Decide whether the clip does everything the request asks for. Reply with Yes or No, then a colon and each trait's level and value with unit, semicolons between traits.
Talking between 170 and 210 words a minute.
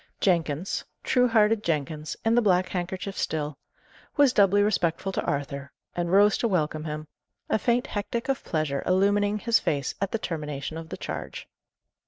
No: average, 160 wpm